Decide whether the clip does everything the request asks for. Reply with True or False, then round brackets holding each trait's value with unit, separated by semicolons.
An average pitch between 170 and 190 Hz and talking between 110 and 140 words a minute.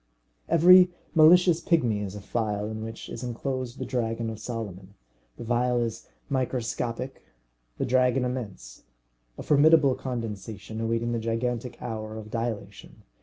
False (115 Hz; 135 wpm)